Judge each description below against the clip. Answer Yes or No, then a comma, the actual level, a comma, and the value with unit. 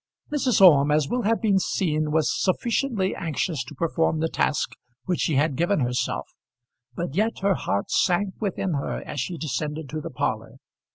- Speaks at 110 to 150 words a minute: No, average, 175 wpm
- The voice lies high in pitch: No, medium, 165 Hz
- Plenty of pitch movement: No, average, 4.6 semitones